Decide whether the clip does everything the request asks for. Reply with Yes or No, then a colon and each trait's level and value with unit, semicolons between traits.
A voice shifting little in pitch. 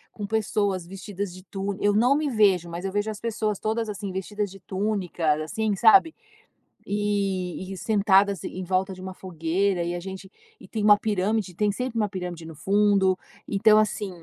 Yes: narrow, 2.1 semitones